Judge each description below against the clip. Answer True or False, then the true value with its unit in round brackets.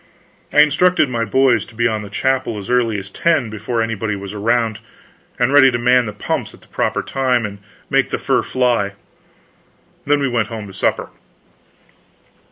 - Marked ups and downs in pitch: False (3.4 semitones)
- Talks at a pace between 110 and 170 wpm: False (185 wpm)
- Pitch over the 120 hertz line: False (115 Hz)